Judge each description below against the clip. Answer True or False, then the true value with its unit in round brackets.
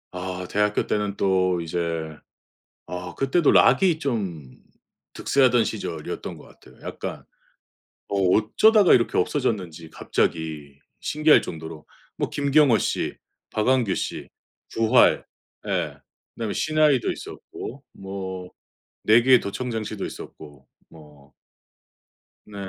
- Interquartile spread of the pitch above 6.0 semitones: True (6.9 semitones)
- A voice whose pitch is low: True (100 Hz)